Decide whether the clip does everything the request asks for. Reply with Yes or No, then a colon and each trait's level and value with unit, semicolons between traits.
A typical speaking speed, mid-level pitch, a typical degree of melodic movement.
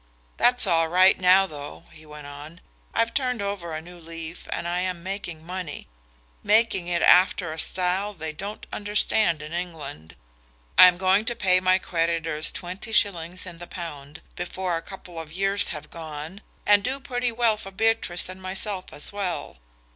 Yes: average, 175 wpm; medium, 180 Hz; average, 3.4 semitones